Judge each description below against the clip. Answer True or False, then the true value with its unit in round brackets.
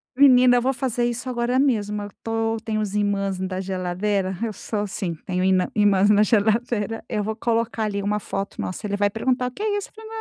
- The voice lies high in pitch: True (215 Hz)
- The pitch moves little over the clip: False (3.2 semitones)